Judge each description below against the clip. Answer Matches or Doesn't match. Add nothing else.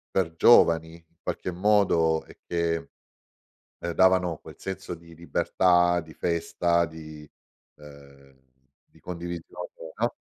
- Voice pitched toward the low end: Matches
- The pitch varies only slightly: Matches